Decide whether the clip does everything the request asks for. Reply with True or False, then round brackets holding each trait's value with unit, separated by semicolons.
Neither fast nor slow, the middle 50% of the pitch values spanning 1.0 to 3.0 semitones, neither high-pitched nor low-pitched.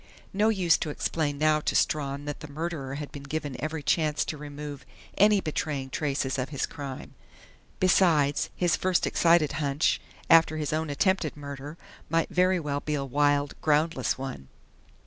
True (165 wpm; 2.4 semitones; 150 Hz)